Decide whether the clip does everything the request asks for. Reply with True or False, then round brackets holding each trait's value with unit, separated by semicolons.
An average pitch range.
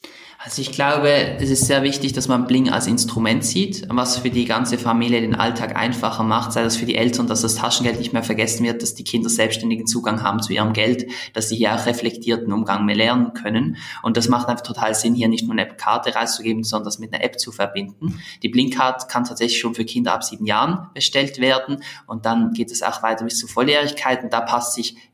False (1.8 semitones)